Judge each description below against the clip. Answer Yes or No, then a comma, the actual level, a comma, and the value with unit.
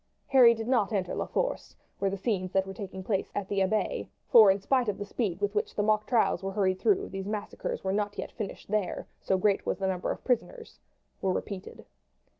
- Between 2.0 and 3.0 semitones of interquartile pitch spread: Yes, narrow, 2.5 semitones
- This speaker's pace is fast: Yes, fast, 225 wpm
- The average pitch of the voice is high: Yes, high, 205 Hz